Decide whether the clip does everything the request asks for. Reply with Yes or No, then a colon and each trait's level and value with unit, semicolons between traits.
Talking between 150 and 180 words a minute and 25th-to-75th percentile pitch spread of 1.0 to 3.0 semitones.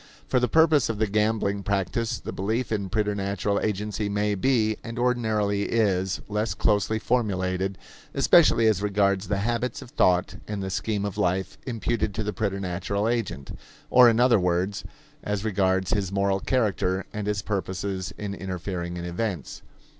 Yes: average, 160 wpm; narrow, 2.5 semitones